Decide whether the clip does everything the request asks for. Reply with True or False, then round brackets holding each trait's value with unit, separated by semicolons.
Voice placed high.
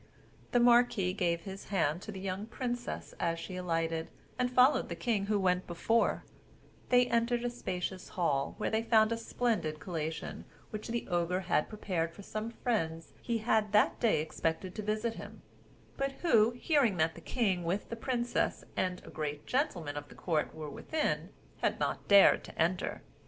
True (200 Hz)